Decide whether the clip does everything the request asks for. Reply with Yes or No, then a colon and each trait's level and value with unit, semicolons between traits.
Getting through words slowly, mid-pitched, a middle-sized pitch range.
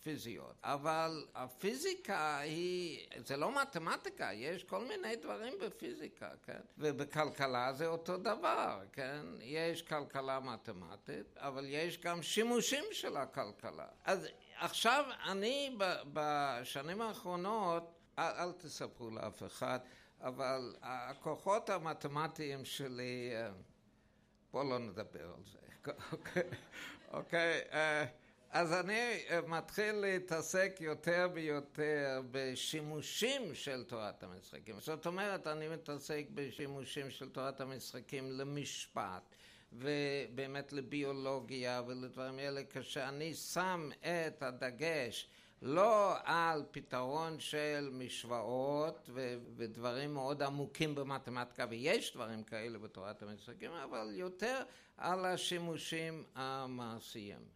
Yes: slow, 95 wpm; medium, 145 Hz; average, 4.4 semitones